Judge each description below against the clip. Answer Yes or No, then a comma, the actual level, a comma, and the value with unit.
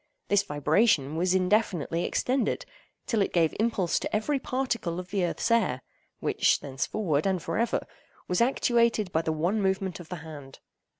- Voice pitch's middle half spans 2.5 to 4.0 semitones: No, average, 5.3 semitones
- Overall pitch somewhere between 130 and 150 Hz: No, medium, 185 Hz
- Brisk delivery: No, average, 165 wpm